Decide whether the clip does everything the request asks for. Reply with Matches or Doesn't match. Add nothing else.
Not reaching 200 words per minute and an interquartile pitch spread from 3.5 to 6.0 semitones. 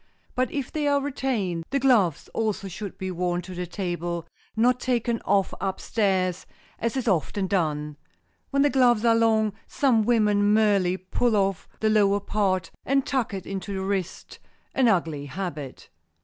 Matches